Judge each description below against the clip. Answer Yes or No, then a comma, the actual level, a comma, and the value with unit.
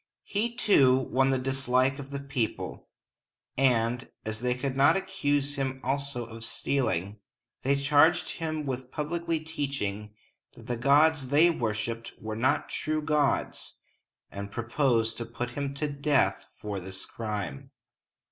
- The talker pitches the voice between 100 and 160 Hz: Yes, low, 135 Hz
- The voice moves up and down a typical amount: Yes, average, 3.8 semitones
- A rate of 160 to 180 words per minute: No, average, 140 wpm